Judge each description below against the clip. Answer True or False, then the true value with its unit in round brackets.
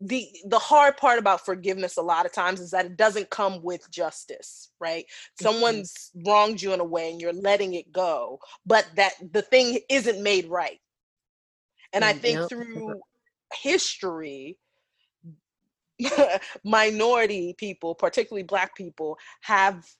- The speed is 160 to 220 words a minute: False (140 wpm)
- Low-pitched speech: False (200 Hz)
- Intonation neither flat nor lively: True (4.3 semitones)